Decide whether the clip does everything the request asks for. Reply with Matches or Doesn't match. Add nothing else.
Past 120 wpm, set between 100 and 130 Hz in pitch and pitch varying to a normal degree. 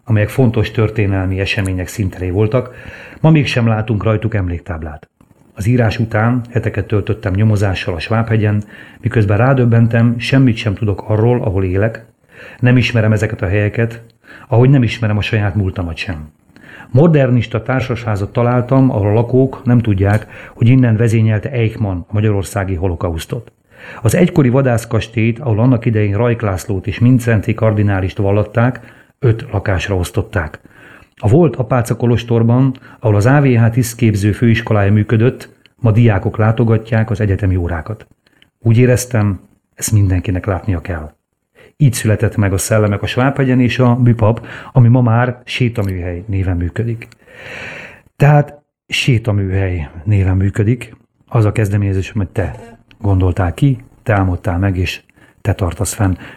Matches